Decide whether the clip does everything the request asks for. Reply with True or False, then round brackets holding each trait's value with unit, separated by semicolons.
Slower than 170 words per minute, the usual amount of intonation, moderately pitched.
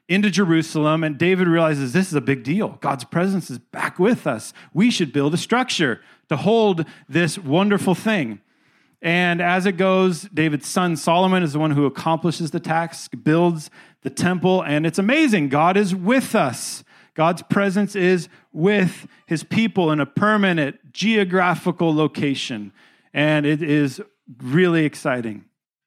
True (155 wpm; 3.7 semitones; 170 Hz)